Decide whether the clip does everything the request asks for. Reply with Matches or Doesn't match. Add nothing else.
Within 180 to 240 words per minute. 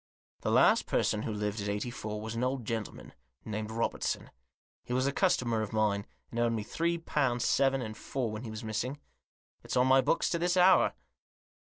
Matches